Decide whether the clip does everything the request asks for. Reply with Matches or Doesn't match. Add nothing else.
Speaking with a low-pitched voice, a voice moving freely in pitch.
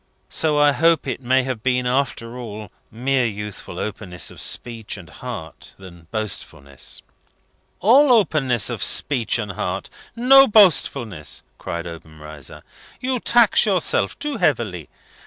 Matches